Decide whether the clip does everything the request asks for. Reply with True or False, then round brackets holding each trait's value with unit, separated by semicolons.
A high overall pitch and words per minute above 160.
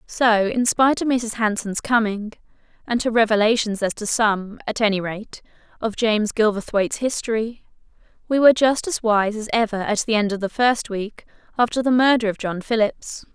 True (220 Hz; 180 wpm)